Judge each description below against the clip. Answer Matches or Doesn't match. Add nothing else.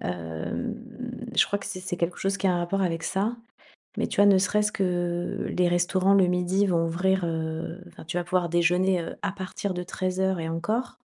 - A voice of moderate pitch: Matches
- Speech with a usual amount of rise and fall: Doesn't match